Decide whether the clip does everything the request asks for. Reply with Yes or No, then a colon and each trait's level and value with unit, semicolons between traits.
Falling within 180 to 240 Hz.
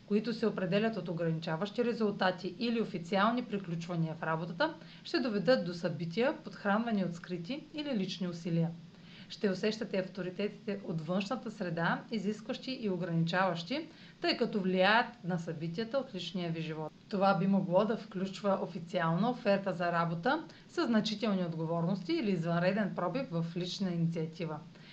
Yes: high, 190 Hz